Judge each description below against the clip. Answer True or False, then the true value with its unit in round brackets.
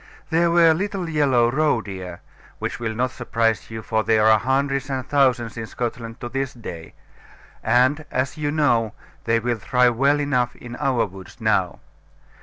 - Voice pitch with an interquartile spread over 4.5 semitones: False (3.8 semitones)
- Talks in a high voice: False (125 Hz)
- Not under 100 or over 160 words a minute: False (170 wpm)